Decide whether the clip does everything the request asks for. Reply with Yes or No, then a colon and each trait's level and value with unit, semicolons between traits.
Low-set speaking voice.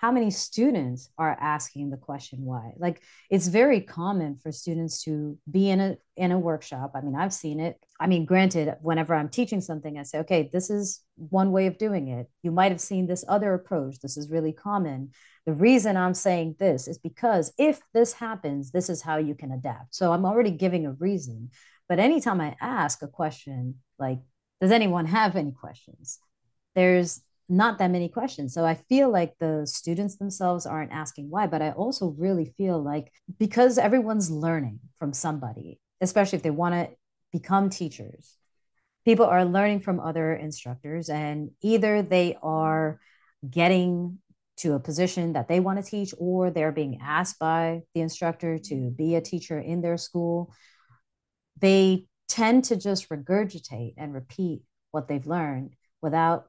No: medium, 170 Hz